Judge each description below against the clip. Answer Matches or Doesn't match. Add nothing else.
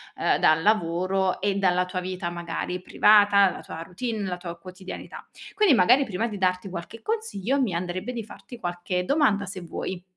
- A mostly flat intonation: Doesn't match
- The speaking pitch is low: Doesn't match